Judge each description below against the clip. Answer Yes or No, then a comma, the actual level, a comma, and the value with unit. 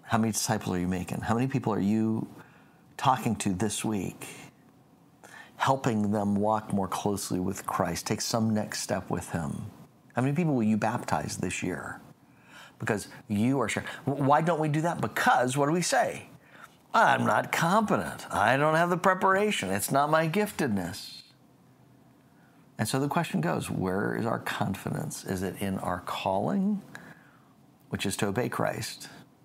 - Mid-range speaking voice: No, low, 125 Hz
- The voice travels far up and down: Yes, wide, 7.0 semitones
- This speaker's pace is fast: No, average, 165 wpm